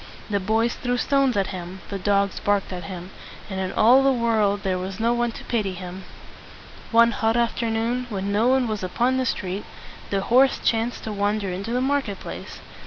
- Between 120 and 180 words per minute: No, average, 195 wpm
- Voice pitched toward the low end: No, high, 215 Hz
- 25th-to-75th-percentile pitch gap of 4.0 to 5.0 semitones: No, average, 3.6 semitones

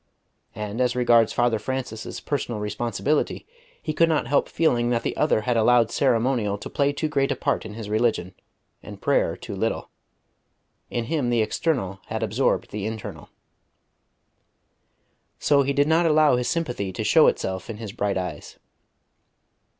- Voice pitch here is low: Yes, low, 120 Hz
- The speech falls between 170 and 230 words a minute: No, average, 160 wpm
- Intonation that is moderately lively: Yes, average, 4.6 semitones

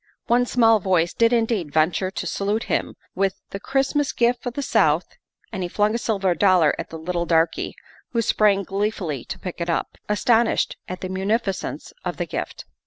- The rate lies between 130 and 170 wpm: No, average, 200 wpm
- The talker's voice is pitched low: No, high, 195 Hz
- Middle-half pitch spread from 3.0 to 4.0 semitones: No, average, 4.5 semitones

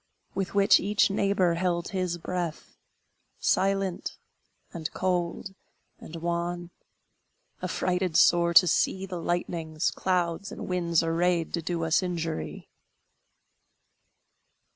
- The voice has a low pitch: No, medium, 175 Hz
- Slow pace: Yes, slow, 105 wpm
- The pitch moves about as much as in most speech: No, narrow, 1.6 semitones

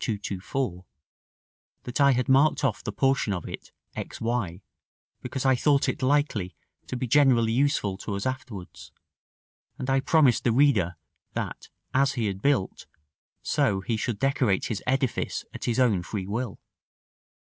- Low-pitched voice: Yes, low, 125 Hz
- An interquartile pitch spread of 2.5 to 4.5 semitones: No, average, 4.9 semitones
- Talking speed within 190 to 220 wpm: No, average, 155 wpm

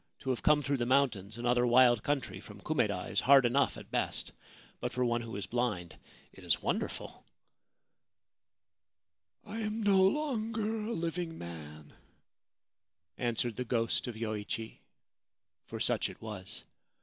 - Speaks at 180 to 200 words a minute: No, average, 150 wpm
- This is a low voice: Yes, low, 125 Hz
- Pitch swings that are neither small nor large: No, wide, 6.2 semitones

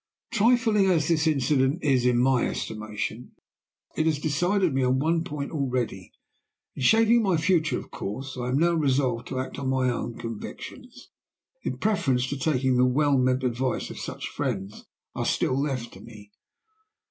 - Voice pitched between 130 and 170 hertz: Yes, low, 135 Hz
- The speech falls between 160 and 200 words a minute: Yes, average, 170 wpm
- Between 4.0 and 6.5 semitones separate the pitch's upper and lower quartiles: Yes, average, 4.3 semitones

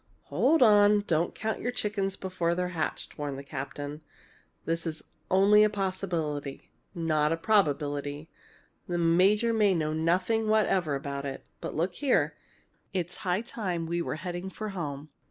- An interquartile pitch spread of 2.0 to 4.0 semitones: No, average, 4.9 semitones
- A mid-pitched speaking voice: Yes, medium, 175 Hz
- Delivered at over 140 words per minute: Yes, average, 155 wpm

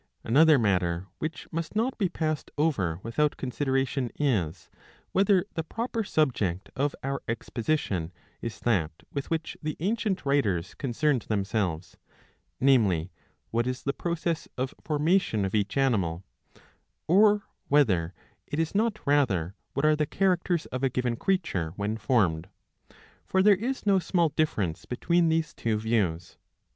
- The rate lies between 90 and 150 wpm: Yes, average, 145 wpm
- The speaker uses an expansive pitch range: Yes, wide, 8.0 semitones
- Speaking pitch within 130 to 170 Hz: Yes, low, 135 Hz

